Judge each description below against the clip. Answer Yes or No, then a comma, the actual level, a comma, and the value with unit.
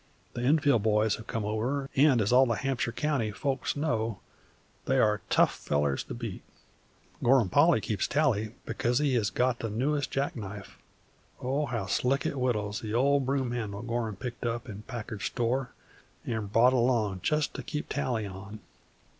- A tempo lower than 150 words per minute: No, average, 170 wpm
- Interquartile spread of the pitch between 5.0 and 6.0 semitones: No, average, 3.8 semitones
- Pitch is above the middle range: No, low, 120 Hz